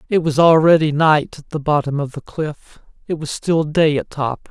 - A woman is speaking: No, male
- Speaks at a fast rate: Yes, fast, 215 wpm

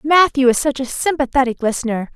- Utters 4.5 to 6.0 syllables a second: Yes, 5.9 syllables/s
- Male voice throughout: No, female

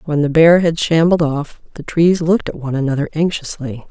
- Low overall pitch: No, medium, 155 Hz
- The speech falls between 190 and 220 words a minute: Yes, average, 200 wpm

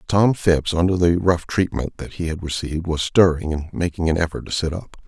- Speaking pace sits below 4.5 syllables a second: No, 5.5 syllables/s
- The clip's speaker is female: No, male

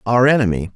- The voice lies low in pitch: Yes, low, 115 Hz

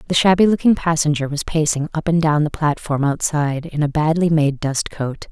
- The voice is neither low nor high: Yes, medium, 155 Hz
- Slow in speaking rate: No, fast, 205 wpm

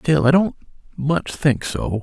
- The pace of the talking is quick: No, average, 180 wpm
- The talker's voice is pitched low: Yes, low, 130 Hz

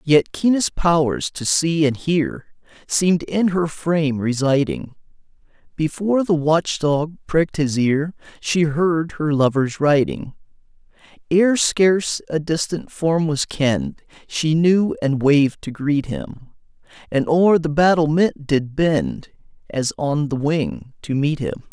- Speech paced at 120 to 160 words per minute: Yes, average, 140 wpm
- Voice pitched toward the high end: No, medium, 155 Hz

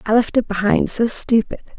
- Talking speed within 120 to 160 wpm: No, average, 200 wpm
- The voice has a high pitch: Yes, high, 220 Hz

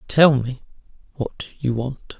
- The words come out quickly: No, slow, 135 wpm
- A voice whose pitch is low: Yes, low, 130 Hz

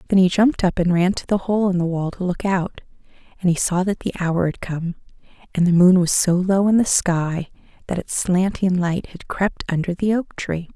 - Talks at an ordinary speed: No, fast, 235 wpm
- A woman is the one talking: Yes, female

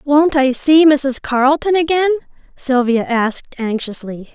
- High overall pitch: Yes, very high, 275 Hz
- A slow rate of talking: Yes, slow, 125 wpm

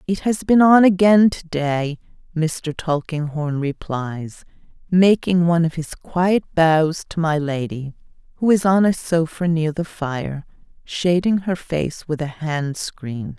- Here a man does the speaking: No, female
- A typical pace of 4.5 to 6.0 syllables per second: No, 3.7 syllables/s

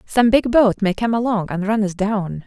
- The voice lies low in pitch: No, high, 210 Hz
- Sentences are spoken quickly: Yes, fast, 245 wpm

